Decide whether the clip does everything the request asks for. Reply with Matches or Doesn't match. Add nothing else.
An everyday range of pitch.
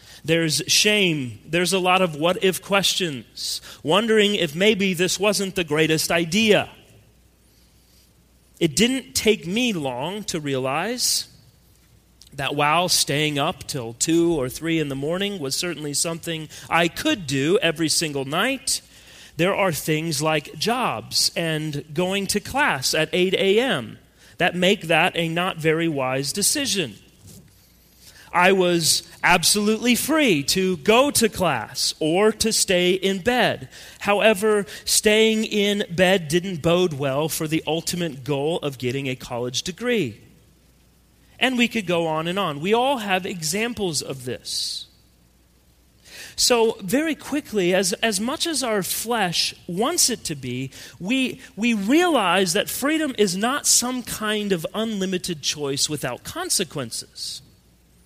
Doesn't match